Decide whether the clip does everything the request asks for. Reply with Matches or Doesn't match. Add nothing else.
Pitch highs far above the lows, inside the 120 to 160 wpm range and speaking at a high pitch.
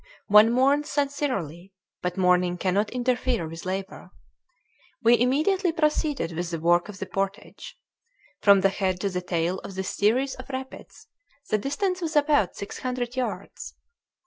Matches